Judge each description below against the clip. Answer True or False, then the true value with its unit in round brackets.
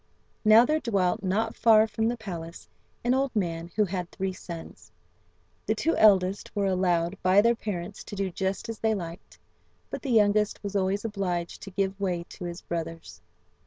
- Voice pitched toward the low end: False (195 Hz)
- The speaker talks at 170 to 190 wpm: True (180 wpm)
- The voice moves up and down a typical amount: True (3.3 semitones)